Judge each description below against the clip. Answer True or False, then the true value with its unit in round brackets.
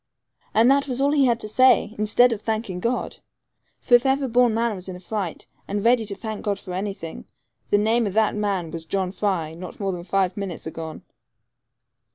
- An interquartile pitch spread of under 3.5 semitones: False (4.1 semitones)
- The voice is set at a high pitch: True (210 Hz)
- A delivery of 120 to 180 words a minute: False (205 wpm)